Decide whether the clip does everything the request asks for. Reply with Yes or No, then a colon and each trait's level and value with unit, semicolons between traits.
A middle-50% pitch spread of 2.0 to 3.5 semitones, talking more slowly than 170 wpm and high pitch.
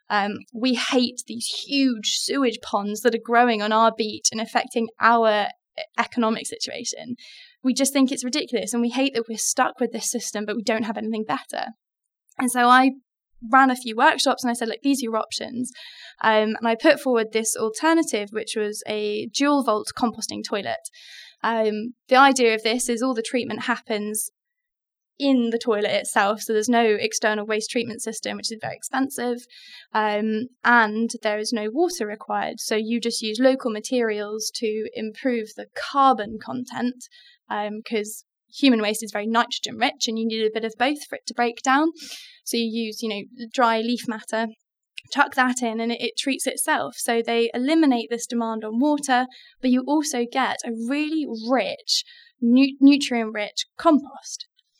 No: average, 3.0 semitones; average, 175 wpm; high, 235 Hz